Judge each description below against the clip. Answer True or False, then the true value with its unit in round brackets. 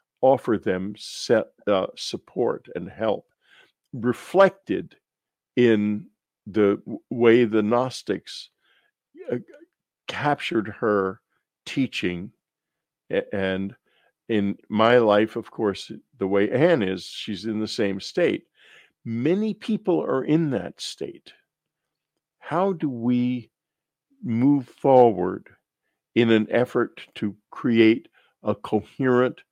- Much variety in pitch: False (4.2 semitones)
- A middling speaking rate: False (100 wpm)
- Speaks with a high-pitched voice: False (115 Hz)